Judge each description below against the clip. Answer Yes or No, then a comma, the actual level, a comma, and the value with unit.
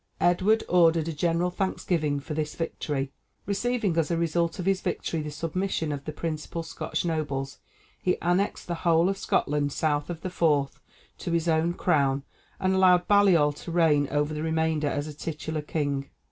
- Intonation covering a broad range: No, average, 2.9 semitones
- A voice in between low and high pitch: Yes, medium, 165 Hz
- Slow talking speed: No, average, 175 wpm